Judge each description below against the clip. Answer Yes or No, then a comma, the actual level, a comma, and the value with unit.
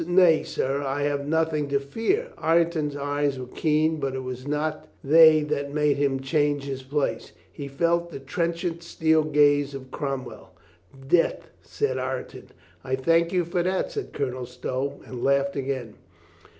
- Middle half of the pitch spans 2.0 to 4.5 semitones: Yes, average, 2.9 semitones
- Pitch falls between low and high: Yes, medium, 145 Hz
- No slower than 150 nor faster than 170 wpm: Yes, average, 165 wpm